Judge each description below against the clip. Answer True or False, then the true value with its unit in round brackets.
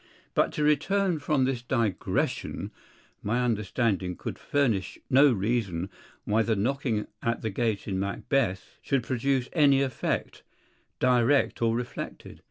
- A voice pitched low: True (120 Hz)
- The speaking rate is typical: False (130 wpm)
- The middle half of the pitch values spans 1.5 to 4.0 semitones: False (4.4 semitones)